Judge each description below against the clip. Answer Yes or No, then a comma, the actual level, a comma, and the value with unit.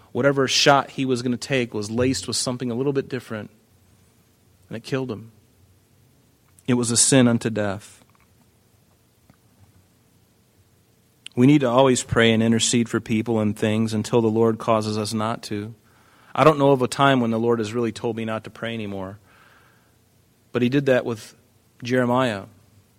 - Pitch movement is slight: Yes, narrow, 2.3 semitones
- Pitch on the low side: Yes, low, 115 Hz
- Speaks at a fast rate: No, average, 170 wpm